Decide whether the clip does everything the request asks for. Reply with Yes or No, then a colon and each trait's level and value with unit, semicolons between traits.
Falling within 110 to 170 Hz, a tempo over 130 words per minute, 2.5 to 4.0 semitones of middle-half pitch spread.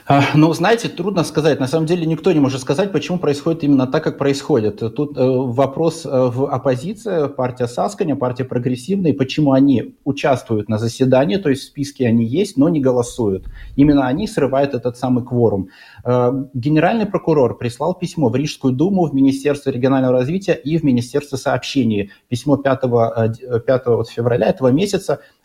Yes: low, 135 Hz; average, 155 wpm; average, 3.7 semitones